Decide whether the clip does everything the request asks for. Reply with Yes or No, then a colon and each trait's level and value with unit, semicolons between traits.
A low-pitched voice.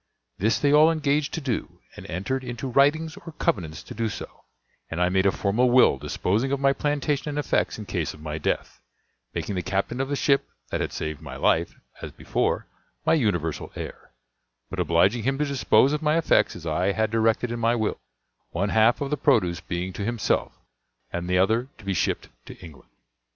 Yes: low, 115 Hz